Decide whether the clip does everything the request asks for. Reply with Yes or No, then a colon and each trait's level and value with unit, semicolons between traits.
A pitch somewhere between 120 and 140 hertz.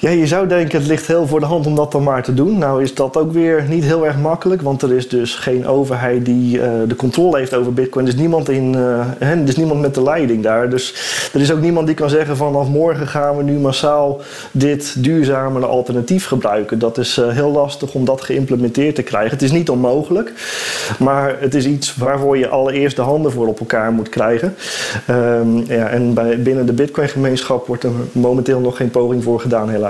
Yes: low, 135 Hz